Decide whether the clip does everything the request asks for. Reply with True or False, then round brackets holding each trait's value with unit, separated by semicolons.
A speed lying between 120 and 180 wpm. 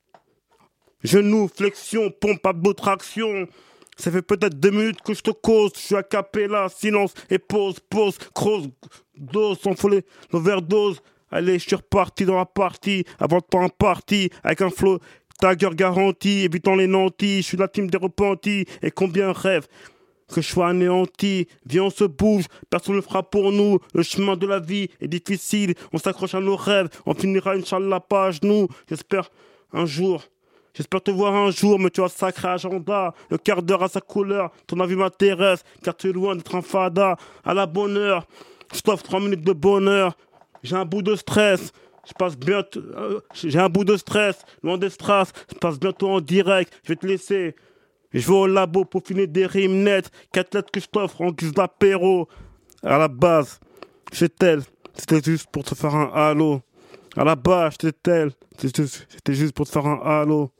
False (190 wpm)